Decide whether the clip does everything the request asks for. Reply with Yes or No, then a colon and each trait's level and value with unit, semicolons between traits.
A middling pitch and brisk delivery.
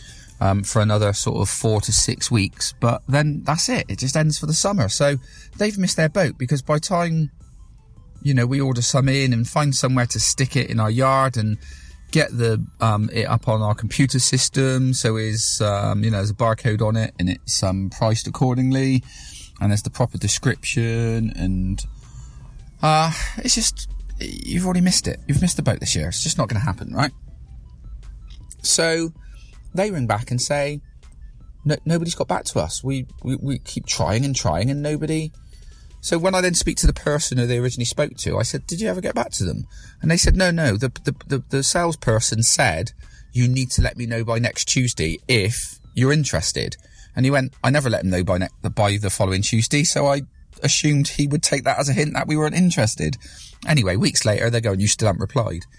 No: low, 125 Hz; fast, 210 wpm